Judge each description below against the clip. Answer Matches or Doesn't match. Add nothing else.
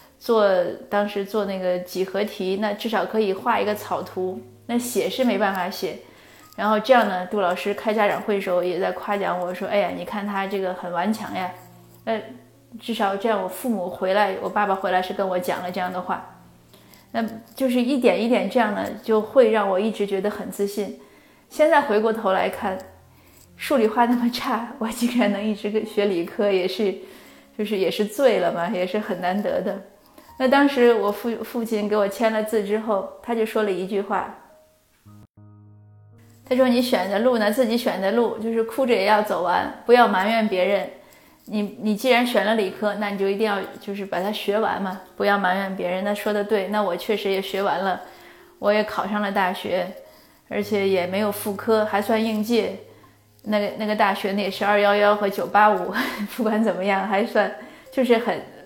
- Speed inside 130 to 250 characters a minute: Doesn't match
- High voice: Matches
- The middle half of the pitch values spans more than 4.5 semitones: Doesn't match